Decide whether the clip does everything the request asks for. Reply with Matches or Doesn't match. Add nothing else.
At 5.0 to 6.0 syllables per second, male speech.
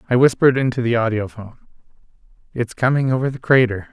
Doesn't match